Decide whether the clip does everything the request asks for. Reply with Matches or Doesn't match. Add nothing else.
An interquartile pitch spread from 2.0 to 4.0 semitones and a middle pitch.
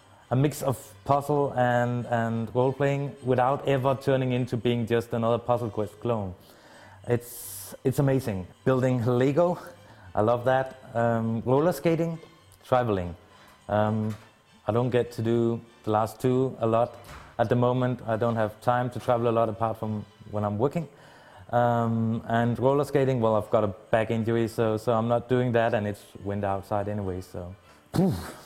Doesn't match